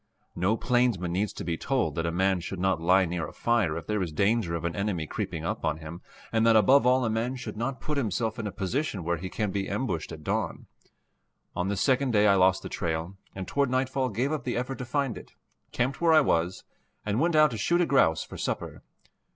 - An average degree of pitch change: No, wide, 6.0 semitones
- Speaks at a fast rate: Yes, fast, 240 wpm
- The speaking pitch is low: Yes, low, 105 Hz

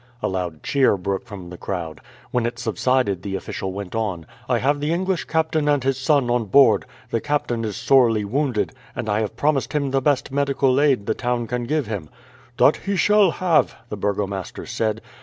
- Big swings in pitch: Yes, wide, 5.7 semitones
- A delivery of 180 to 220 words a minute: Yes, average, 195 wpm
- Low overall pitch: Yes, low, 120 Hz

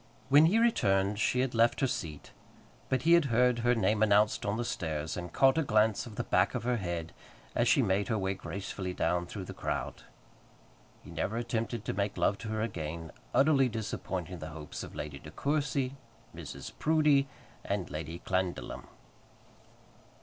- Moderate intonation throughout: No, wide, 5.9 semitones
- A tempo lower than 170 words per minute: No, average, 175 wpm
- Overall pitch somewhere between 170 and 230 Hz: No, low, 105 Hz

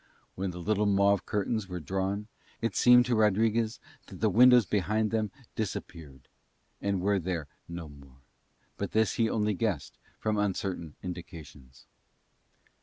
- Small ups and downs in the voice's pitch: No, average, 3.9 semitones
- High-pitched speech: No, low, 100 Hz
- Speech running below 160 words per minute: Yes, average, 140 wpm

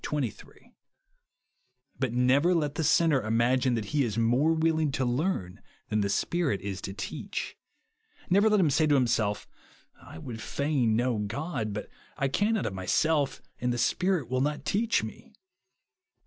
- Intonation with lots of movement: Yes, wide, 6.0 semitones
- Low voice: Yes, low, 130 Hz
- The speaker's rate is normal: Yes, average, 160 wpm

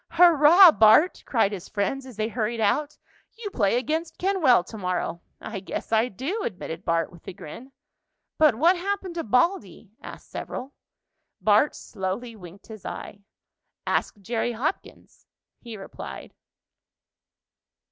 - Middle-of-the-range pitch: No, high, 235 Hz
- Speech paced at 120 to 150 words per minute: Yes, slow, 135 wpm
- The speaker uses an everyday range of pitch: No, wide, 7.5 semitones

